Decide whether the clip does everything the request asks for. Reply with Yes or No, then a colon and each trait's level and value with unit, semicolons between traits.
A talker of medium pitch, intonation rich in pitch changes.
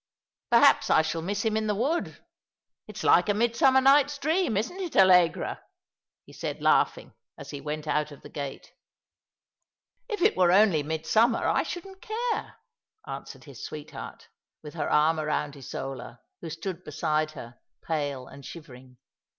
Yes: medium, 170 Hz; wide, 7.9 semitones